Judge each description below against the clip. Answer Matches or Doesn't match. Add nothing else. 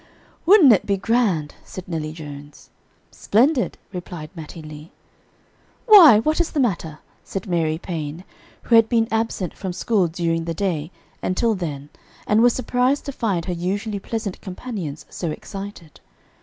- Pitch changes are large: Matches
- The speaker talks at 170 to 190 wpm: Doesn't match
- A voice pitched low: Doesn't match